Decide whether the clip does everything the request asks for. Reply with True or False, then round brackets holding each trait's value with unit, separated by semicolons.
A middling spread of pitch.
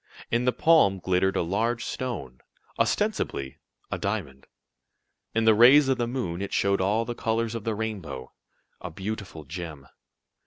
True (5.0 semitones)